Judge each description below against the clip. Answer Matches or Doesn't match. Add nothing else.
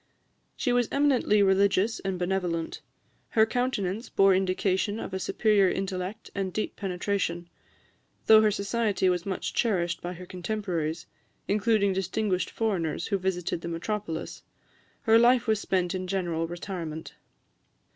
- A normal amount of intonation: Matches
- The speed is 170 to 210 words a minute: Doesn't match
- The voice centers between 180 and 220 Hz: Matches